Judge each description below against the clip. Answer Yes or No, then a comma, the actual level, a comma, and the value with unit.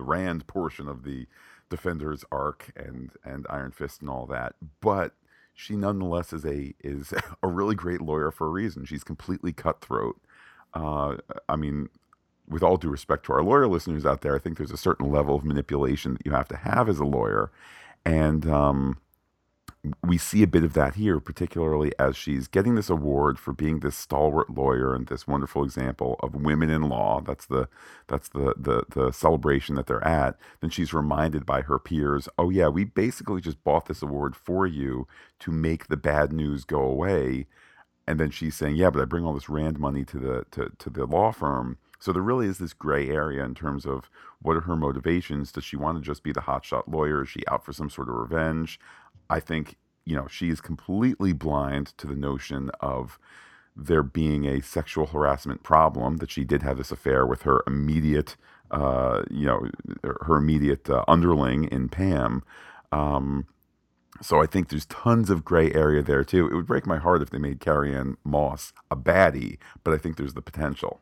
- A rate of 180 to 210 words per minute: Yes, average, 200 wpm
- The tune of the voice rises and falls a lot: No, average, 2.8 semitones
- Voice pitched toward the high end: No, very low, 75 Hz